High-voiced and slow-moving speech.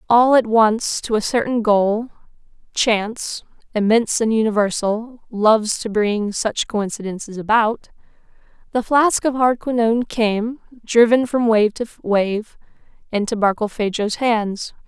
Yes: high, 220 Hz; slow, 115 wpm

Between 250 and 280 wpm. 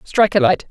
Yes: fast, 255 wpm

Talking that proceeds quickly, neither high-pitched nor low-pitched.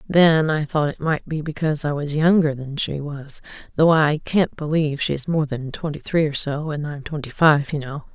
Yes: fast, 230 wpm; medium, 150 Hz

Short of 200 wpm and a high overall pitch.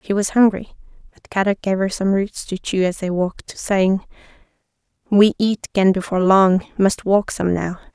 Yes: average, 180 wpm; high, 195 Hz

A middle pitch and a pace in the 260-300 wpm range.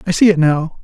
Yes: medium, 165 Hz; fast, 285 wpm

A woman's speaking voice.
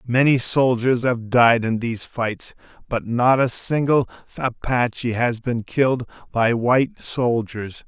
No: male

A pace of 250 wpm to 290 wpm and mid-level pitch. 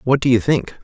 No: fast, 285 wpm; low, 125 Hz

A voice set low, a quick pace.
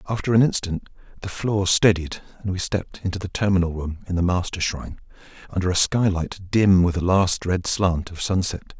No: very low, 90 Hz; average, 185 wpm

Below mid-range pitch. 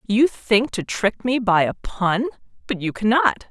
No: high, 210 Hz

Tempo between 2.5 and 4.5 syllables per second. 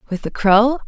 No: 4.8 syllables/s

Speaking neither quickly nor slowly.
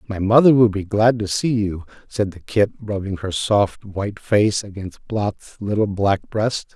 Yes: average, 185 wpm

